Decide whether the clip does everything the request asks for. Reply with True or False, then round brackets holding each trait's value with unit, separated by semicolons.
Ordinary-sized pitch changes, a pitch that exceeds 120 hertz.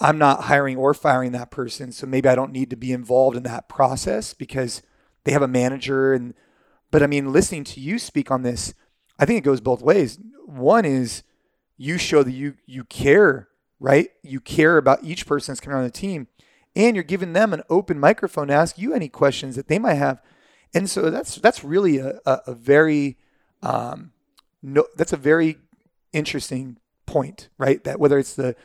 True (3.2 semitones; 140 Hz)